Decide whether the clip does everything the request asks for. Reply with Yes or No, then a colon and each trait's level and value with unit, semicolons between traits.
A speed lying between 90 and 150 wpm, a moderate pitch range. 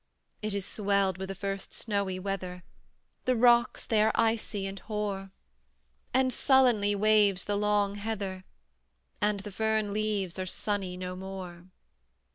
No: average, 140 wpm; narrow, 1.9 semitones